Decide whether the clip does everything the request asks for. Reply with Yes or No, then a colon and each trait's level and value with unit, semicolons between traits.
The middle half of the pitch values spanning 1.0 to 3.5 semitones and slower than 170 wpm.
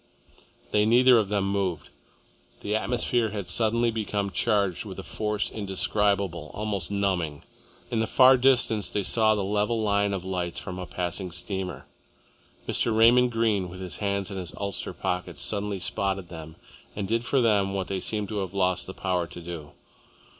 No: average, 2.9 semitones; average, 175 wpm